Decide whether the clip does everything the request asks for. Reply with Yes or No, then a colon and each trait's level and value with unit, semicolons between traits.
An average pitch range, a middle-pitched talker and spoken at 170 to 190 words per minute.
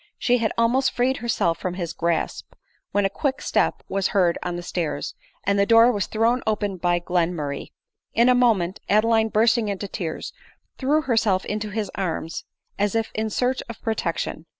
No: average, 4.5 semitones; high, 205 Hz; average, 175 wpm